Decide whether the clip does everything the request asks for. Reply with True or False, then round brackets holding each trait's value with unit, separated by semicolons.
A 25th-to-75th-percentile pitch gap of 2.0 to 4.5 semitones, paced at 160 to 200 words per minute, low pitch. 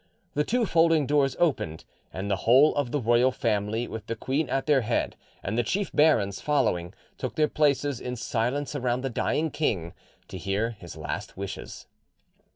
False (5.5 semitones; 175 wpm; 125 Hz)